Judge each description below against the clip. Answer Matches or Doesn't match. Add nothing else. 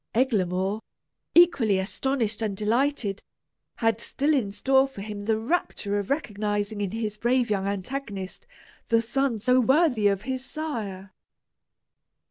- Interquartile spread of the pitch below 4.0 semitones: Doesn't match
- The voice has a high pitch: Matches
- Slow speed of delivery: Matches